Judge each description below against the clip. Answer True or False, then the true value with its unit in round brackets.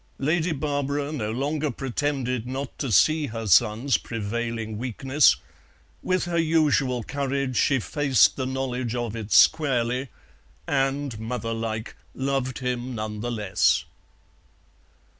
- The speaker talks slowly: True (120 wpm)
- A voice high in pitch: False (130 Hz)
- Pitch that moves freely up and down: False (3.6 semitones)